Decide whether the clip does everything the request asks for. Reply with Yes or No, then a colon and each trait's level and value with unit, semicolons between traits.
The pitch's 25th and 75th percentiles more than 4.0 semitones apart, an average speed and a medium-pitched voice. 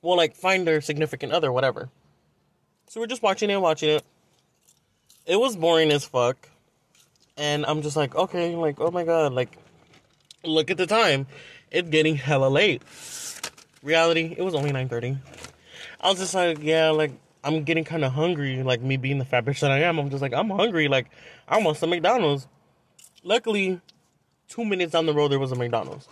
No: average, 3.7 semitones; average, 190 wpm; medium, 155 Hz